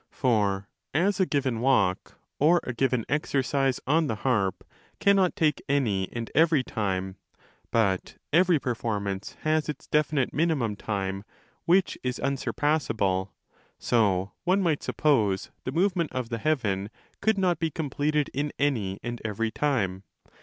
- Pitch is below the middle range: Yes, low, 130 Hz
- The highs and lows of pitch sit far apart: Yes, wide, 6.9 semitones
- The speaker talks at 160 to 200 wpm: No, average, 140 wpm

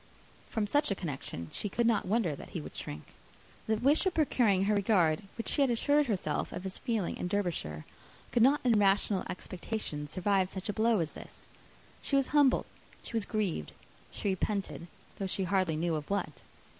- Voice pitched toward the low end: No, high, 200 Hz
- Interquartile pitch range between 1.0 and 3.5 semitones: No, average, 4.6 semitones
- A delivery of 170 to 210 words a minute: Yes, average, 190 wpm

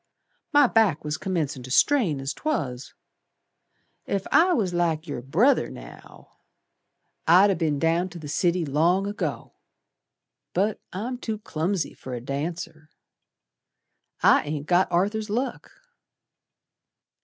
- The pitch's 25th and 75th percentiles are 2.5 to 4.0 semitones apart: No, wide, 5.4 semitones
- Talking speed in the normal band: No, slow, 125 wpm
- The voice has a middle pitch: Yes, medium, 175 Hz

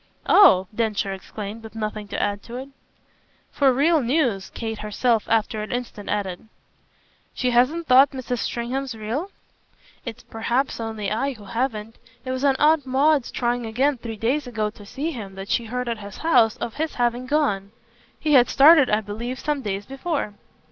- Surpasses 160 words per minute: Yes, average, 175 wpm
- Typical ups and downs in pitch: Yes, average, 4.0 semitones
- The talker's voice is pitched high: Yes, high, 240 Hz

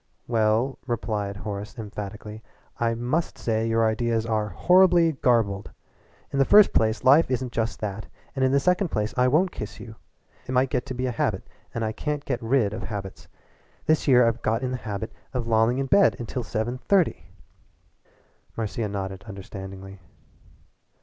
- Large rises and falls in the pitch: No, average, 3.4 semitones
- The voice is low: Yes, low, 115 Hz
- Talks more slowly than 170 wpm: No, average, 175 wpm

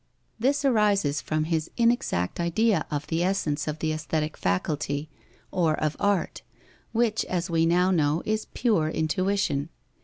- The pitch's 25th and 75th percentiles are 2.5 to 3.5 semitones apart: No, average, 4.8 semitones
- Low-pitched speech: No, medium, 165 Hz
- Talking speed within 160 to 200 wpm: No, average, 145 wpm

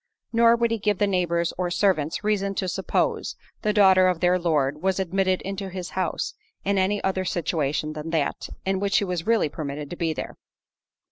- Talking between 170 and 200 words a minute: Yes, average, 195 wpm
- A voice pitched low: No, medium, 185 Hz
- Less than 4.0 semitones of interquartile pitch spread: Yes, average, 3.0 semitones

